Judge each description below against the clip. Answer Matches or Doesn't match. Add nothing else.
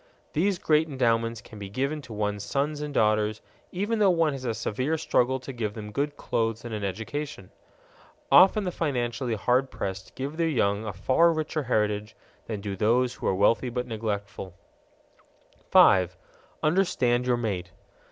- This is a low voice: Matches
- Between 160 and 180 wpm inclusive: Matches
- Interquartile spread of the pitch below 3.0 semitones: Doesn't match